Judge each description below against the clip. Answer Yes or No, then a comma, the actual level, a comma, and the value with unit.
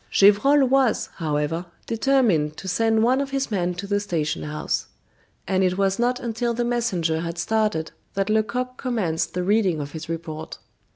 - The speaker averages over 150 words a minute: Yes, average, 170 wpm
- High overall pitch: Yes, high, 200 Hz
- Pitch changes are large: Yes, wide, 6.1 semitones